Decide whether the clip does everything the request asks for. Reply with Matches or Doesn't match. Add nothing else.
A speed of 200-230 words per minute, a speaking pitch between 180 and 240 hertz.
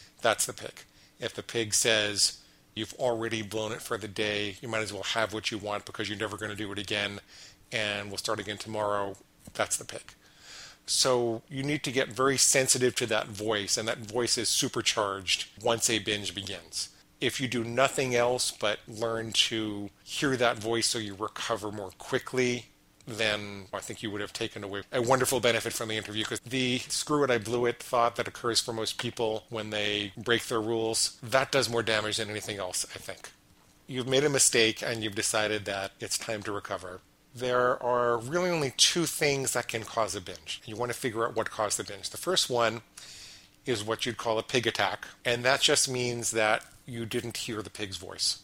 Doesn't match